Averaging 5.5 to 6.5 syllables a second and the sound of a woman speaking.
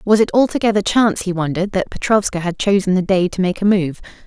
Yes: 6.3 syllables/s; female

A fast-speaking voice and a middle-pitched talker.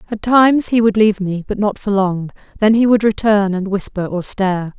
No: fast, 225 wpm; high, 205 Hz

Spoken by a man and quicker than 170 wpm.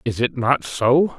Yes: male; fast, 205 wpm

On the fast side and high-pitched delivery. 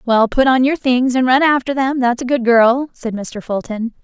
Yes: fast, 240 wpm; very high, 250 Hz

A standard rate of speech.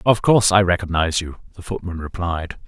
Yes: average, 180 wpm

